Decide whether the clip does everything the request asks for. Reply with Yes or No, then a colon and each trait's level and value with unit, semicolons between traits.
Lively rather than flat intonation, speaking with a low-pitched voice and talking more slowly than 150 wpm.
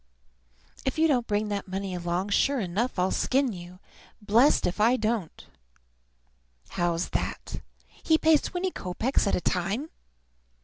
No: wide, 6.4 semitones; high, 210 Hz; average, 140 wpm